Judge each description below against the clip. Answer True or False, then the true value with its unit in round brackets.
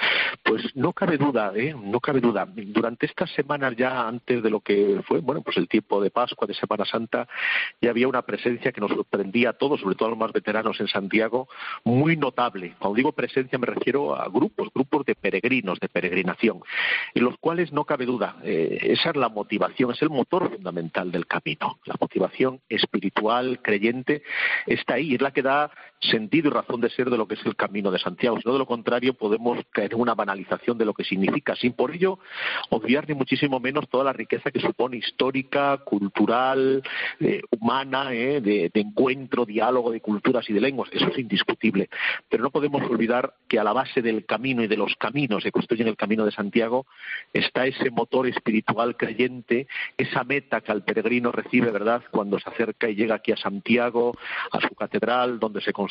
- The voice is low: True (120 Hz)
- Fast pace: True (200 wpm)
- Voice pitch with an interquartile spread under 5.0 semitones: True (3.4 semitones)